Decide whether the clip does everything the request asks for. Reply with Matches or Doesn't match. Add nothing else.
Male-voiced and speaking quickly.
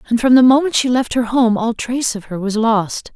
Doesn't match